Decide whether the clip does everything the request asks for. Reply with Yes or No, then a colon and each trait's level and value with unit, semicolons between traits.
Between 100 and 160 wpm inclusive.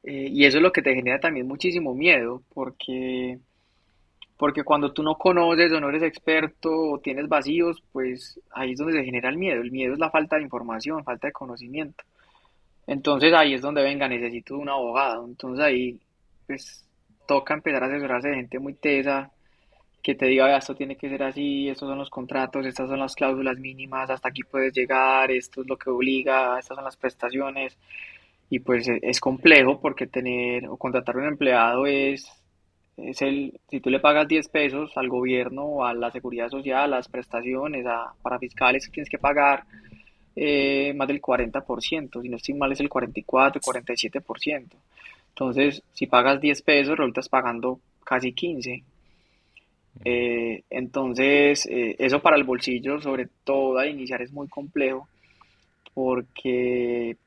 No: average, 170 wpm